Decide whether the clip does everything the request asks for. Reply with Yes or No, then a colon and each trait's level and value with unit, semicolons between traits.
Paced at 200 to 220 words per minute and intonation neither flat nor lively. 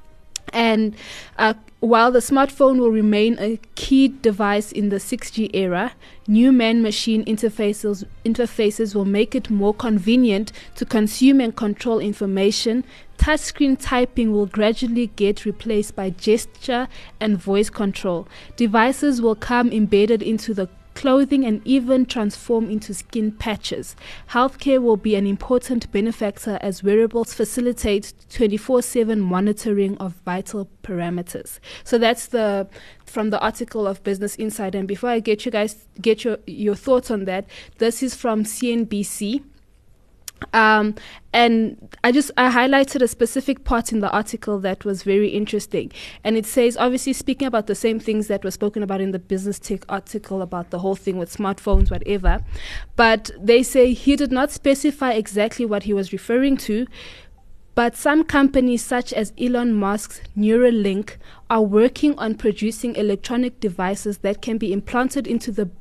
No: average, 155 wpm; average, 3.0 semitones